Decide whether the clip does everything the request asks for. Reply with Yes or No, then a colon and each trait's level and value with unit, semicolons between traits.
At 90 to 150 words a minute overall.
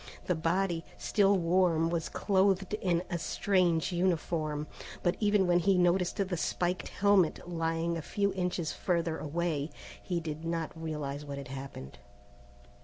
Yes: average, 145 wpm